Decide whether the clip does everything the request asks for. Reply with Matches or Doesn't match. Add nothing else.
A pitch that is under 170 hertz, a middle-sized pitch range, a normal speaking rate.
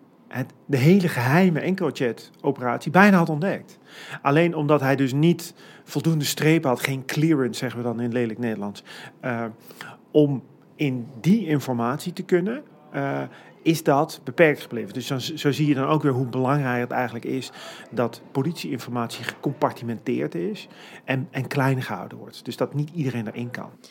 Matches